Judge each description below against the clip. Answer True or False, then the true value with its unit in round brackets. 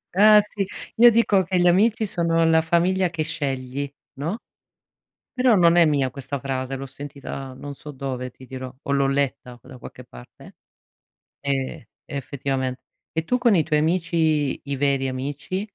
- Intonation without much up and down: False (4.6 semitones)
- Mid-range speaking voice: True (145 Hz)